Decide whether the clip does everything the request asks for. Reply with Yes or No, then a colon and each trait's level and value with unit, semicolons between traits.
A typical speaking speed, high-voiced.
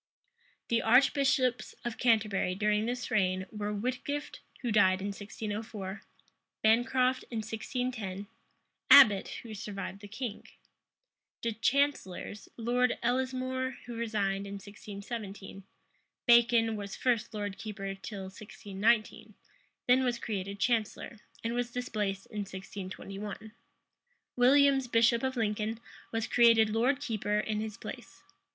No: slow, 120 wpm; high, 220 Hz